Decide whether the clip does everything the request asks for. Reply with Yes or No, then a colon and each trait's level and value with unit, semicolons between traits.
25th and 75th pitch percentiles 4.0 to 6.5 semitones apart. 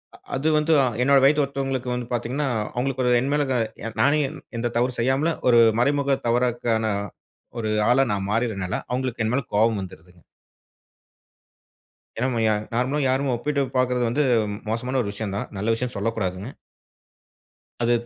No: average, 3.3 semitones